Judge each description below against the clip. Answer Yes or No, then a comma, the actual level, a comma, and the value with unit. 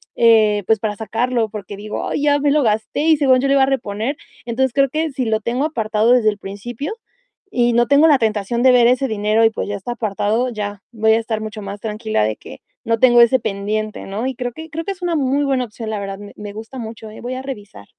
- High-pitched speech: Yes, high, 230 Hz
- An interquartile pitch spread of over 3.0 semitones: Yes, average, 3.5 semitones